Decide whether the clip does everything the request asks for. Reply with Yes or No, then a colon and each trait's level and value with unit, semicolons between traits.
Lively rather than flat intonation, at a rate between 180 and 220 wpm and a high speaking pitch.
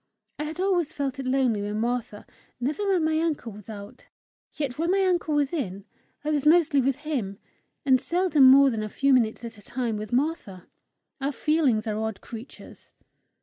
Yes: wide, 5.8 semitones; average, 190 wpm; very high, 265 Hz